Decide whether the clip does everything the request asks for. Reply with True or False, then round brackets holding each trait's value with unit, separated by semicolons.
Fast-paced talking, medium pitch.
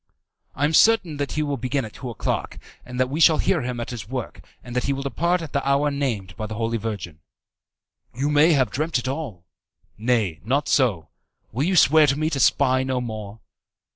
False (210 wpm; 130 Hz)